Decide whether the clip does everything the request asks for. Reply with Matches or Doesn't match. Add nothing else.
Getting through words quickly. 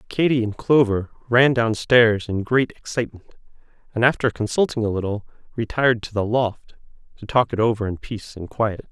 Doesn't match